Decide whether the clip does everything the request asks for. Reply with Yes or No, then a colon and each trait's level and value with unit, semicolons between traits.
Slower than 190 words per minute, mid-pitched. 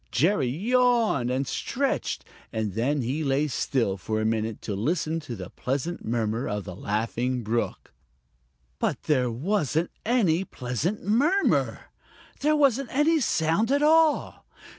Yes: average, 140 wpm; medium, 145 Hz